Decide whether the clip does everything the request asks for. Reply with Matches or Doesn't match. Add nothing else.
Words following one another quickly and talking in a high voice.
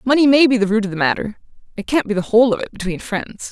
Matches